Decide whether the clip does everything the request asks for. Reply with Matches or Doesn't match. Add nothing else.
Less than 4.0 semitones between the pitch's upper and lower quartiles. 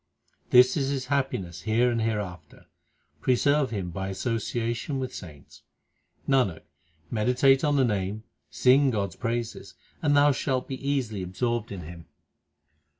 Doesn't match